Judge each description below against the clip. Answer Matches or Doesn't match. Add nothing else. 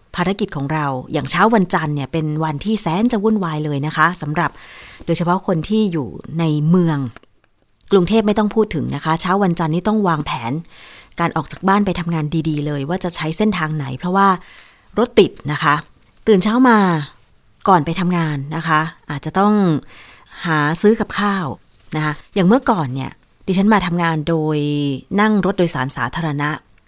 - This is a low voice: Doesn't match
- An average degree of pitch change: Matches